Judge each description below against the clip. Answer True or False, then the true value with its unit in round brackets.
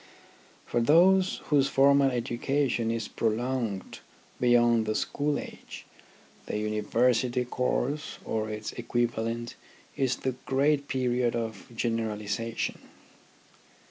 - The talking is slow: True (100 wpm)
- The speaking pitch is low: True (120 Hz)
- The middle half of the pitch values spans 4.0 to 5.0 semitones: False (2.9 semitones)